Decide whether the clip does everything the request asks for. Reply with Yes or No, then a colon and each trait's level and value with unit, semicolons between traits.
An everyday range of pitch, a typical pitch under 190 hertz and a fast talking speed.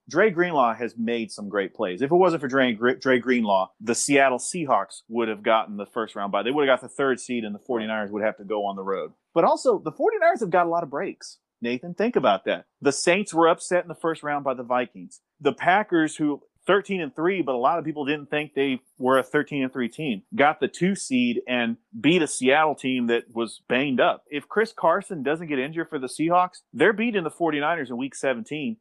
No: wide, 6.3 semitones; medium, 140 Hz; fast, 240 wpm